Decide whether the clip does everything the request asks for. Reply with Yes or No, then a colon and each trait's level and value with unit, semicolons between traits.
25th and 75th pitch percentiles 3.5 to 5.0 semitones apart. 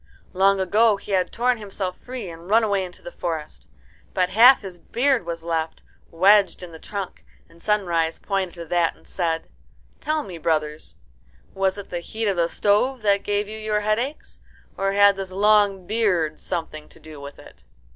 Yes: average, 3.8 semitones